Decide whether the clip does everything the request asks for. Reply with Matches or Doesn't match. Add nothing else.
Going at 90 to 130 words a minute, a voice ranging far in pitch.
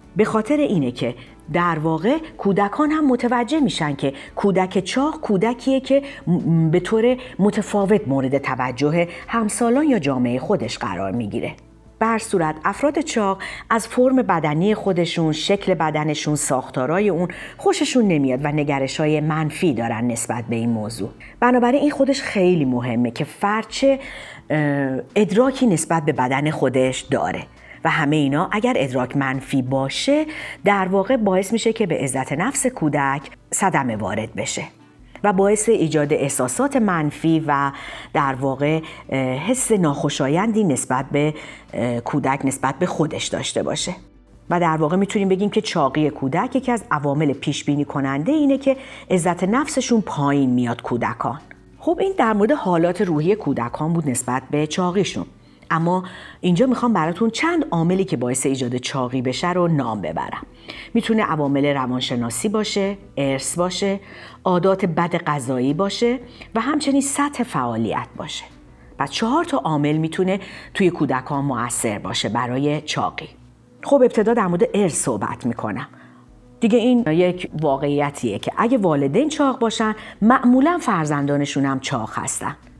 Doesn't match